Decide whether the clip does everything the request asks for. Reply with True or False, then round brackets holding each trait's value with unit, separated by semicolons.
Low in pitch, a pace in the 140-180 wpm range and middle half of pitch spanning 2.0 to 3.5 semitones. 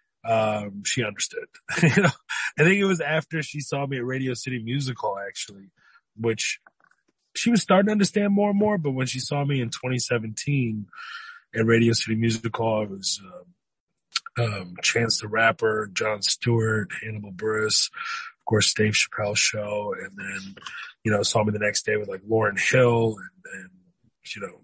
False (115 Hz; 175 wpm; 4.8 semitones)